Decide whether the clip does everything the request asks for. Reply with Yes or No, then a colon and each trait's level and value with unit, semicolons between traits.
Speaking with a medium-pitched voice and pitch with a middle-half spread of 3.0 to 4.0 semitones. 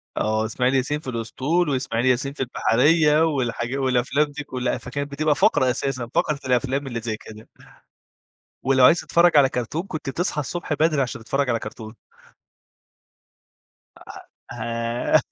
No: low, 130 Hz; average, 3.7 semitones